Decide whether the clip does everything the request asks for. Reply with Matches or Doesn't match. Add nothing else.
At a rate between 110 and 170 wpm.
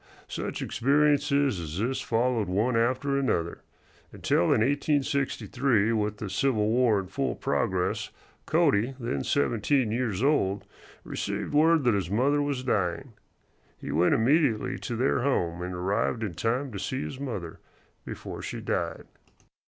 Matches